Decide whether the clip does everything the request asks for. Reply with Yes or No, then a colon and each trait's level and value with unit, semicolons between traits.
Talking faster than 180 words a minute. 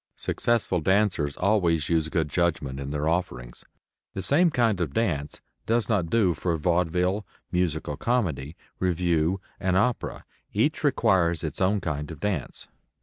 No: average, 145 wpm